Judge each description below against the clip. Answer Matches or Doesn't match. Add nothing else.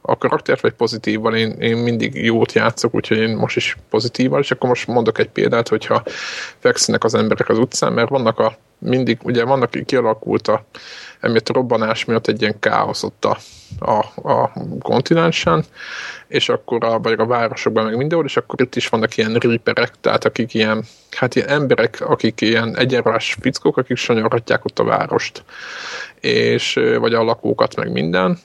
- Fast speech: Matches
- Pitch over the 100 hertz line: Matches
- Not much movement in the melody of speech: Matches